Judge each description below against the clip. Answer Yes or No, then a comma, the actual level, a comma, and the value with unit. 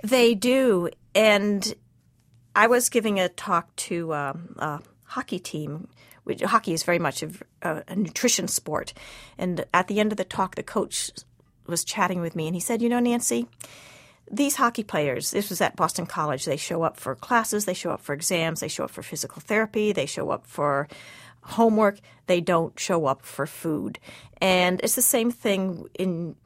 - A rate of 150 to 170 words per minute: No, average, 185 wpm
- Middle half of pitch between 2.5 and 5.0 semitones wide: No, wide, 5.4 semitones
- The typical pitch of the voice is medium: Yes, medium, 180 Hz